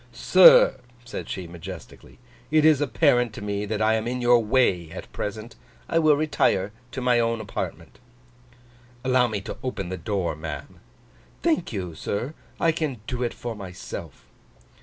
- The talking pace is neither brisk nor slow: Yes, average, 160 wpm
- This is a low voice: Yes, low, 115 Hz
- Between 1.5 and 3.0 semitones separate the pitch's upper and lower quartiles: No, average, 5.0 semitones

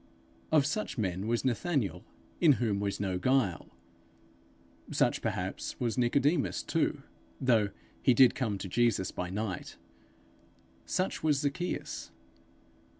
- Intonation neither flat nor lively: No, wide, 5.8 semitones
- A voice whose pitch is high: No, low, 120 Hz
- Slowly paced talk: Yes, slow, 120 wpm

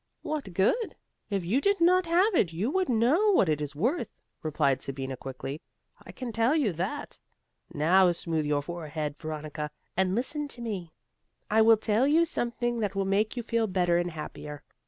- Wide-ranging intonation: Yes, wide, 8.0 semitones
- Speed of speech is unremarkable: Yes, average, 180 wpm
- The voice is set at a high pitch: Yes, high, 195 Hz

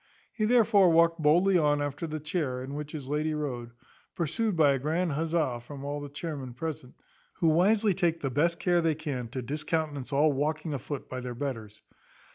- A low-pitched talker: No, medium, 150 Hz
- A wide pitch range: No, average, 3.3 semitones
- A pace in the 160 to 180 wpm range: No, average, 190 wpm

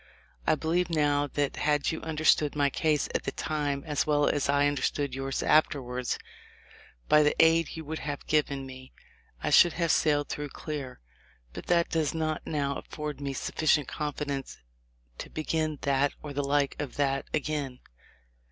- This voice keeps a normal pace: Yes, average, 170 wpm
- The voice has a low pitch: No, medium, 145 Hz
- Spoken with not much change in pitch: Yes, narrow, 1.7 semitones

